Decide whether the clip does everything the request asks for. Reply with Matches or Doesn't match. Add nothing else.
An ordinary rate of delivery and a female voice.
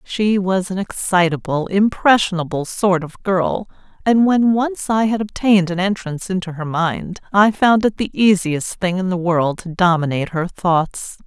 Matches